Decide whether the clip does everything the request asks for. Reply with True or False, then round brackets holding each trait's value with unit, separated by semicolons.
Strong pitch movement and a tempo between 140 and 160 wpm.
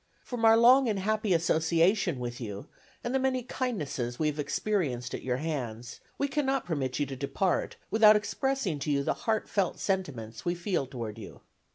False (8.9 semitones; 180 wpm)